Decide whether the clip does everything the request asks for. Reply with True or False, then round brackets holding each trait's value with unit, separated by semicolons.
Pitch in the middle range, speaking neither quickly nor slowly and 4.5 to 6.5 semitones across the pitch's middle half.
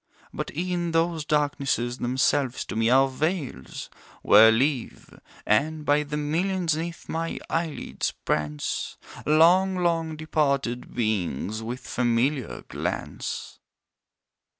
False (145 Hz; 105 wpm; 5.2 semitones)